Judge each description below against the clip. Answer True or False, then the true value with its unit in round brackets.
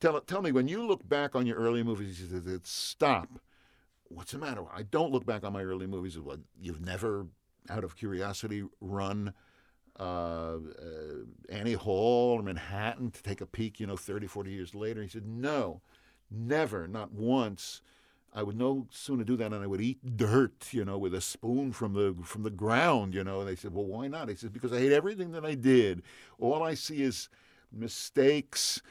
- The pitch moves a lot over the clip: False (4.7 semitones)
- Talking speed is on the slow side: False (205 wpm)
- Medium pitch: False (110 Hz)